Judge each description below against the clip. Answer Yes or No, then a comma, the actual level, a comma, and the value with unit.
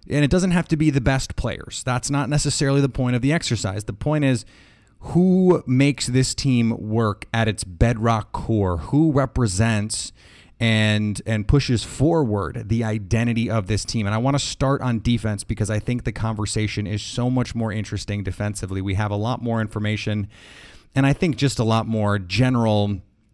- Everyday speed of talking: Yes, average, 185 wpm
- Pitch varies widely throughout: No, average, 4.0 semitones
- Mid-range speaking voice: No, low, 115 Hz